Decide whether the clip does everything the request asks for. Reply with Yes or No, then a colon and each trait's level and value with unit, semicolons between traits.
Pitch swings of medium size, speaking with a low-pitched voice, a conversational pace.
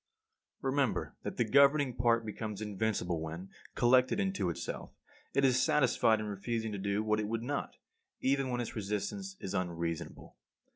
Yes: average, 4.6 semitones; low, 110 Hz; average, 160 wpm